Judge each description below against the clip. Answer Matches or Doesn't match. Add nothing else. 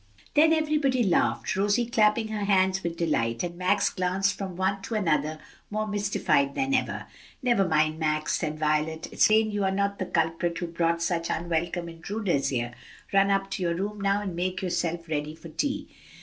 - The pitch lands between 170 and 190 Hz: Matches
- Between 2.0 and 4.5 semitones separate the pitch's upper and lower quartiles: Matches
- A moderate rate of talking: Matches